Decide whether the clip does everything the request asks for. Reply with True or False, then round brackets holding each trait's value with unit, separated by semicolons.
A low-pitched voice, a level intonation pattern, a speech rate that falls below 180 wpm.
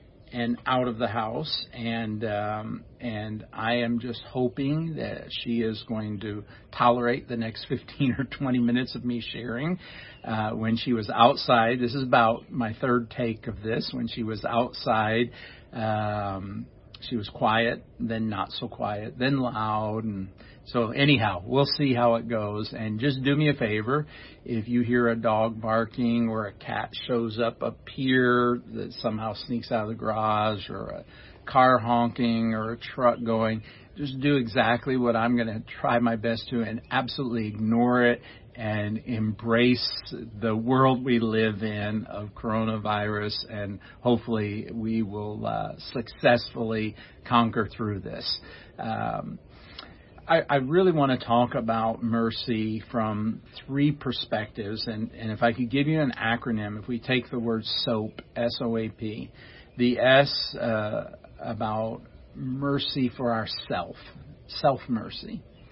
True (115 Hz; 1.9 semitones; 155 wpm)